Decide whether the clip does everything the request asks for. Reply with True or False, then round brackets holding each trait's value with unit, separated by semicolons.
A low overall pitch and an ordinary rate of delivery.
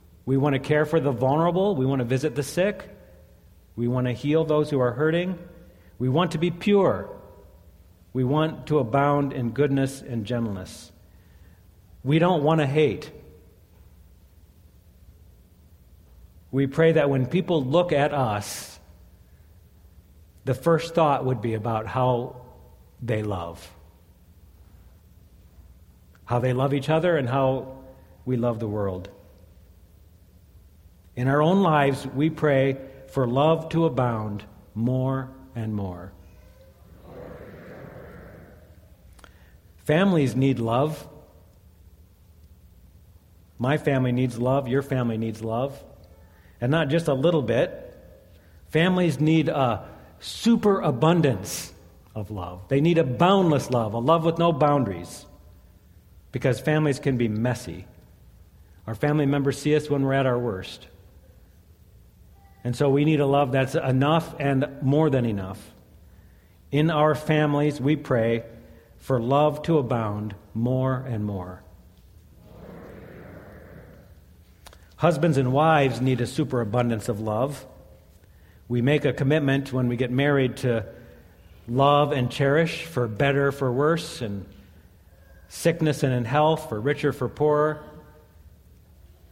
False (120 Hz; 125 wpm)